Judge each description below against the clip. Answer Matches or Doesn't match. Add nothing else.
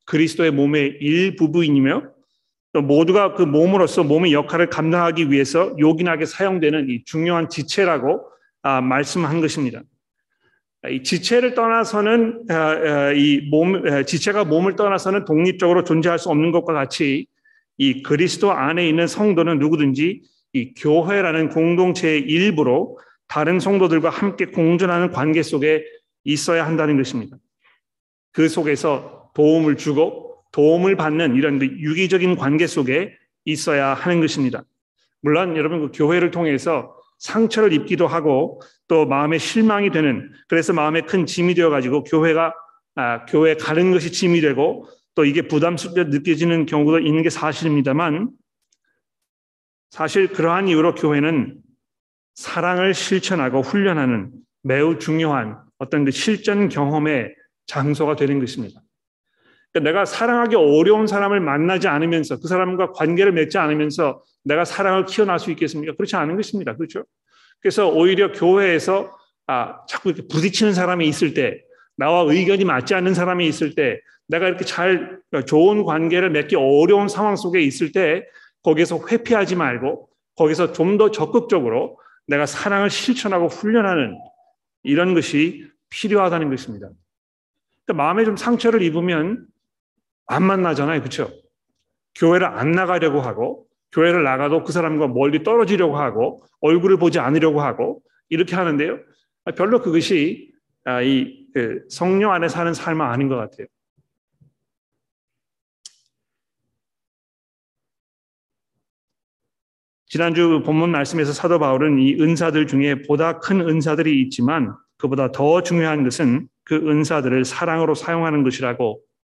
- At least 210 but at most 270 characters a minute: Doesn't match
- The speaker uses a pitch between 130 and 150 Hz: Doesn't match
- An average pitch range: Matches